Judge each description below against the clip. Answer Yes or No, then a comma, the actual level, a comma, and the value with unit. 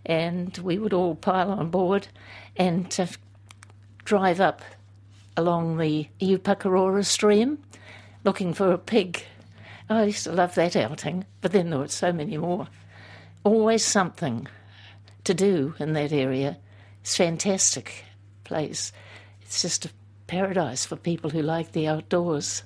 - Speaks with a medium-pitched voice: Yes, medium, 160 Hz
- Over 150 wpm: No, average, 145 wpm